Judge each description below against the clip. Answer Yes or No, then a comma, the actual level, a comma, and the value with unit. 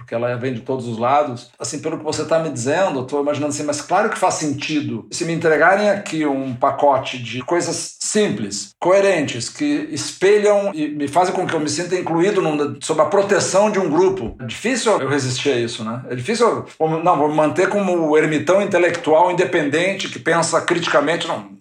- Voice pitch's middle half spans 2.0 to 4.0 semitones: No, average, 4.4 semitones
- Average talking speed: No, fast, 205 wpm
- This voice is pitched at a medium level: Yes, medium, 155 Hz